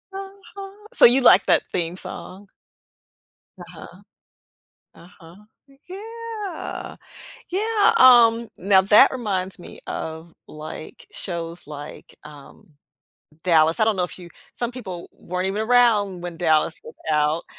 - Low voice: No, high, 190 Hz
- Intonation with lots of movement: Yes, wide, 6.6 semitones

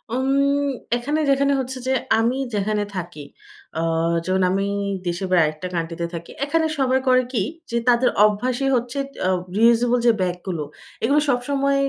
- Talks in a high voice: Yes, high, 240 Hz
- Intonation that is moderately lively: No, wide, 6.0 semitones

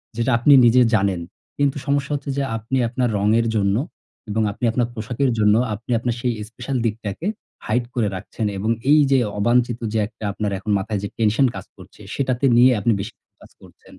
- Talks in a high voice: No, low, 115 Hz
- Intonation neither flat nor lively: Yes, average, 3.2 semitones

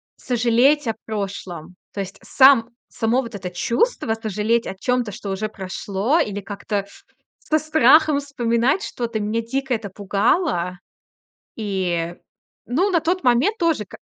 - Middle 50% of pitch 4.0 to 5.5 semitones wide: Yes, average, 5.0 semitones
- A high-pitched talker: Yes, high, 230 Hz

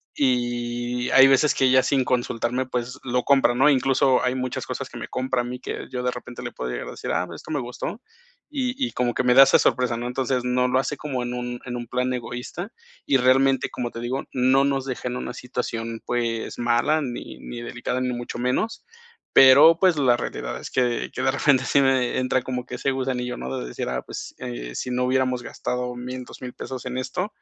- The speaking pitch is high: No, low, 125 Hz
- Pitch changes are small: Yes, narrow, 1.4 semitones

